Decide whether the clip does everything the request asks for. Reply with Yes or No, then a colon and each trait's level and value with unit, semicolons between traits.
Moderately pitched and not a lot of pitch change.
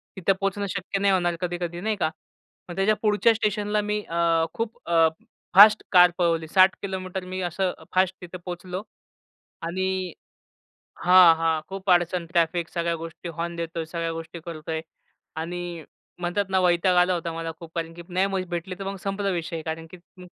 Yes: medium, 180 Hz; narrow, 2.2 semitones